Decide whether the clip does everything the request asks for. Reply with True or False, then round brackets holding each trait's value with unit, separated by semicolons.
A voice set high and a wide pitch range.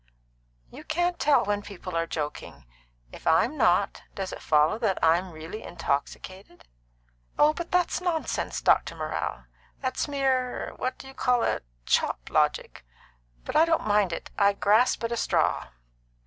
True (210 Hz; 7.5 semitones)